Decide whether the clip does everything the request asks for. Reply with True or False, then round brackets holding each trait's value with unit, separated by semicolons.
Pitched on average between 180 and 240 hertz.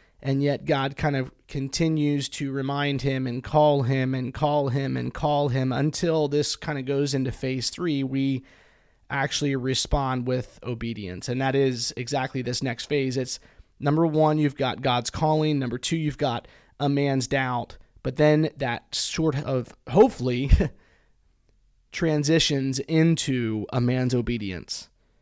False (135 Hz)